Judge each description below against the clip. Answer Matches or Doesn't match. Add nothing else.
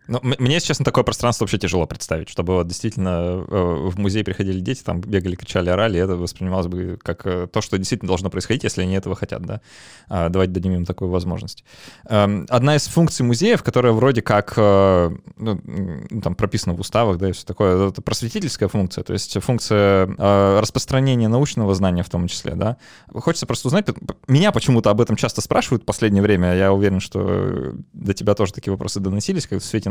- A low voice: Matches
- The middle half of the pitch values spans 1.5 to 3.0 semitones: Doesn't match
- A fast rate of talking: Matches